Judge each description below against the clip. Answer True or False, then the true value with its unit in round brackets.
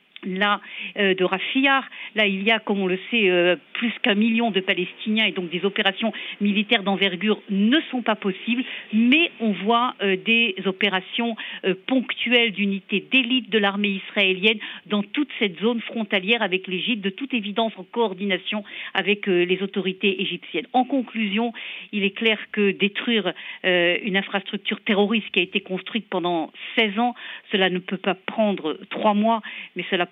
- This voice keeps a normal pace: True (170 wpm)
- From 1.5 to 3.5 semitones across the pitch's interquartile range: True (3.0 semitones)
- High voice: True (205 Hz)